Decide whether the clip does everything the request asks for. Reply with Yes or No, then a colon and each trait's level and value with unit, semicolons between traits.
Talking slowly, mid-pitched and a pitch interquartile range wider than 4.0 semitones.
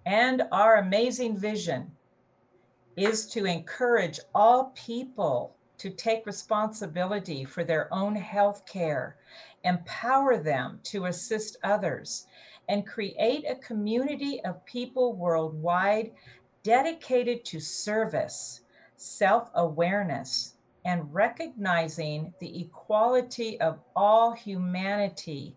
No: slow, 95 wpm; high, 205 Hz; average, 4.9 semitones